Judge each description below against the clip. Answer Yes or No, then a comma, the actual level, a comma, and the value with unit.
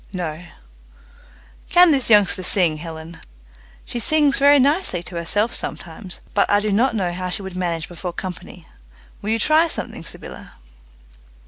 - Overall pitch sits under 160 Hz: No, high, 190 Hz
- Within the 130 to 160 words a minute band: Yes, average, 150 wpm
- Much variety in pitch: Yes, wide, 5.8 semitones